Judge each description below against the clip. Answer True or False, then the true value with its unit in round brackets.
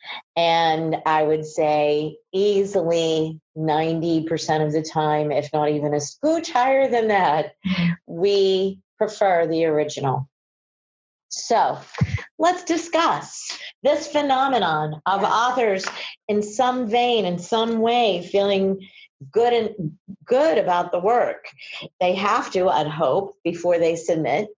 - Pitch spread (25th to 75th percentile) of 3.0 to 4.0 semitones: False (5.3 semitones)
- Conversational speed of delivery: False (120 wpm)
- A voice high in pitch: False (180 Hz)